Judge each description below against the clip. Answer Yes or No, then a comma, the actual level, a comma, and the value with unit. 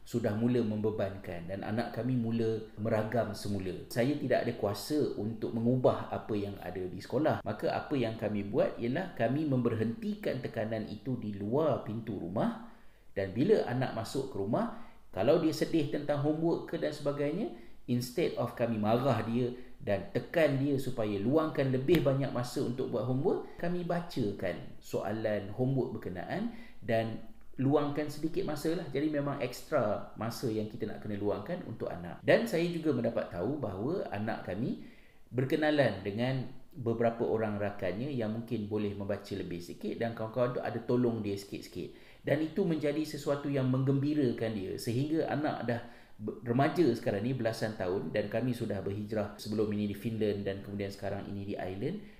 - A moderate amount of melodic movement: Yes, average, 4.6 semitones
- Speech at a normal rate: No, fast, 160 wpm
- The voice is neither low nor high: No, low, 115 Hz